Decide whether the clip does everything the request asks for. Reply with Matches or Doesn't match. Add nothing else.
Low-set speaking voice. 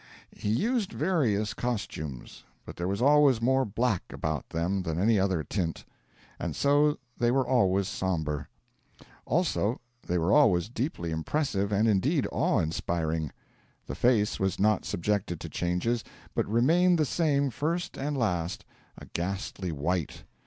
Matches